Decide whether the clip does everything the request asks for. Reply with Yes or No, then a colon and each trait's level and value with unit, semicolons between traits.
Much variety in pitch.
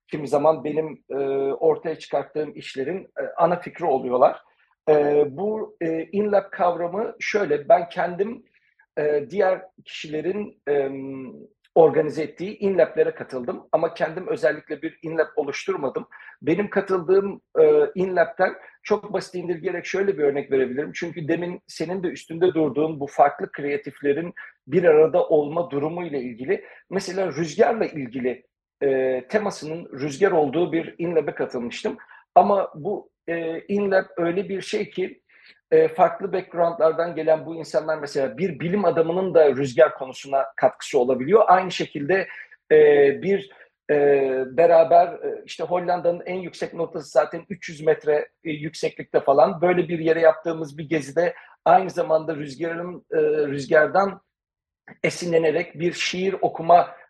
No: average, 4.0 semitones